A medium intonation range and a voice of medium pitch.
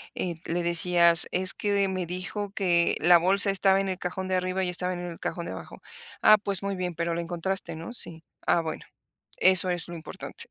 No: narrow, 1.9 semitones; medium, 180 Hz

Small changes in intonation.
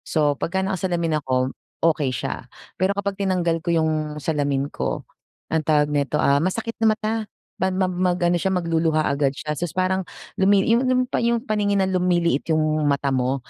No: average, 4.1 semitones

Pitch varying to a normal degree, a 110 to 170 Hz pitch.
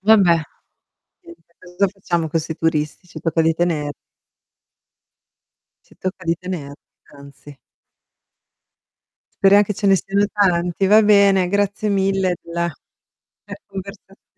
No: average, 3.2 semitones; medium, 185 Hz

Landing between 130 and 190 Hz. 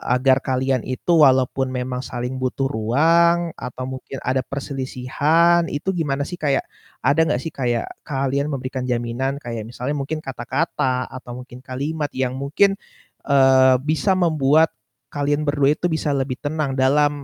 Yes: low, 135 Hz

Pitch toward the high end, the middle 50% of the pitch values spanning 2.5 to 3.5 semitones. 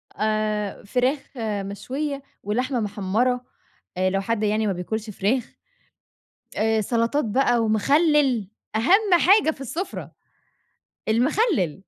No: high, 230 Hz; average, 4.7 semitones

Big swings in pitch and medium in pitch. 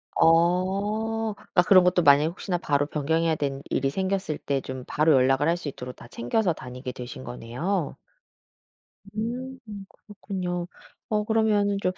Yes: wide, 6.2 semitones; medium, 175 Hz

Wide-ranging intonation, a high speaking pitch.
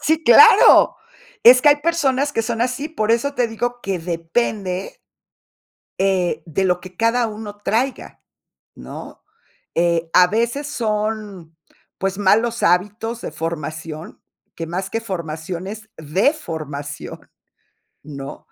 Yes: wide, 5.9 semitones; high, 205 Hz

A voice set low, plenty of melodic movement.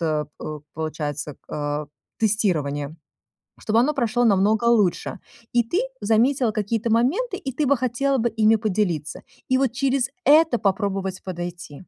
No: high, 220 Hz; wide, 6.0 semitones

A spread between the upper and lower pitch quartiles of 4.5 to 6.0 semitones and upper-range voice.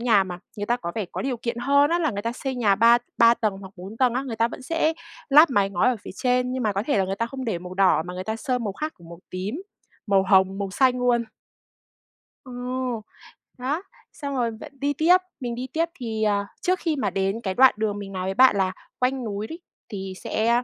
Yes: average, 4.8 semitones; high, 230 Hz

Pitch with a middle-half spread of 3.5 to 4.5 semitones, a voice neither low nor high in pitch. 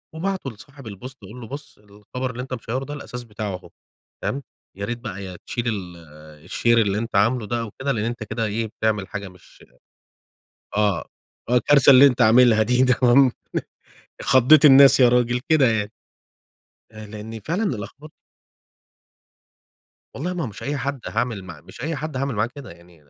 No: average, 4.1 semitones; low, 120 Hz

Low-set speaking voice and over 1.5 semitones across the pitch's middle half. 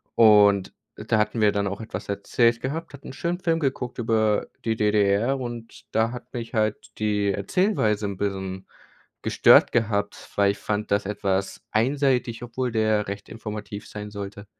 Yes: low, 110 Hz; average, 2.7 semitones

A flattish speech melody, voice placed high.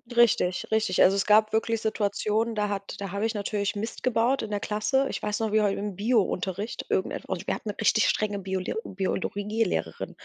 Yes: narrow, 1.8 semitones; high, 210 Hz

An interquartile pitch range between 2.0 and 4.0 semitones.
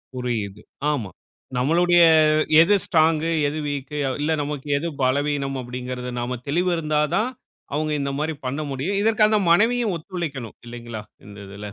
No: average, 5.1 semitones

